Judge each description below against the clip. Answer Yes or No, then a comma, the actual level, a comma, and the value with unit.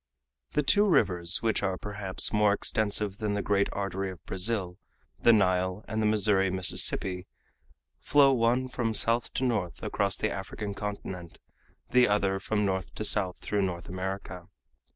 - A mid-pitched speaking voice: No, low, 100 Hz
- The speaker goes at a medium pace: Yes, average, 155 wpm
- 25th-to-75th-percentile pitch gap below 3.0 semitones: Yes, narrow, 2.6 semitones